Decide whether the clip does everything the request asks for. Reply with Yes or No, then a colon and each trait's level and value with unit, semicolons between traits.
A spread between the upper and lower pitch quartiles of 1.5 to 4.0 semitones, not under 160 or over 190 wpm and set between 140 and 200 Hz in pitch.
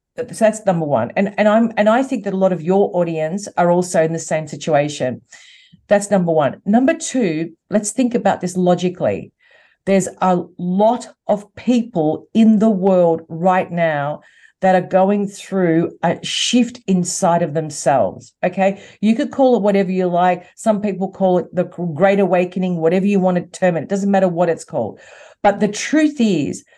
Yes: average, 3.3 semitones; average, 185 wpm; high, 190 Hz